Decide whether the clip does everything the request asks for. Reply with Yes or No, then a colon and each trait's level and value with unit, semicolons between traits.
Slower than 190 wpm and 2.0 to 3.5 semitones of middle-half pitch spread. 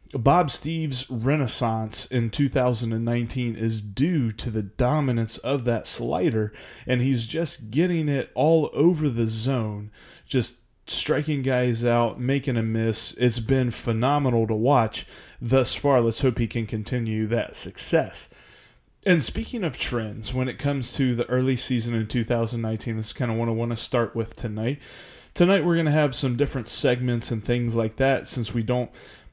Yes: average, 170 wpm; average, 2.9 semitones